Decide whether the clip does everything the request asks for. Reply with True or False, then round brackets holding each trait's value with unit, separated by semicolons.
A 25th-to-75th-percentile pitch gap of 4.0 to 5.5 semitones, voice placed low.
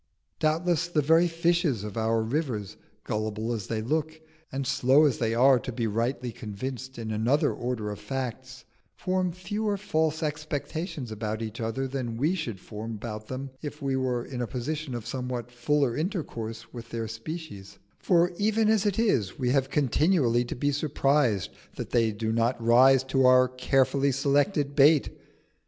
True (5.0 semitones; 130 Hz)